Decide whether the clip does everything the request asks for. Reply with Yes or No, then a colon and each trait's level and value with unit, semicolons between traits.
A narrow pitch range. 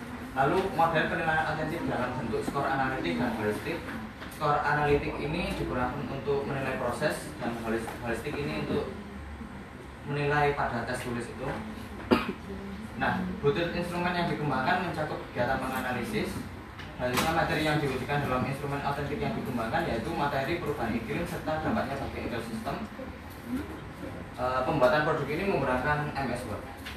No: average, 3.6 semitones